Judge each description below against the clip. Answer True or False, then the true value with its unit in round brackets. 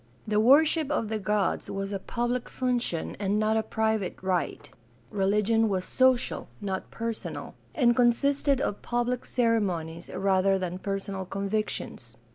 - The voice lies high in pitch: True (215 Hz)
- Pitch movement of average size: True (3.7 semitones)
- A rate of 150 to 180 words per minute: False (135 wpm)